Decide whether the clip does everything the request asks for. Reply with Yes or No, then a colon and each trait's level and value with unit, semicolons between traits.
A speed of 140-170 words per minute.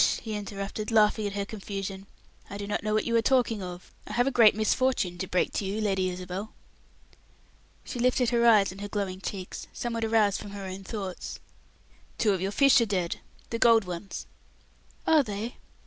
No: average, 195 wpm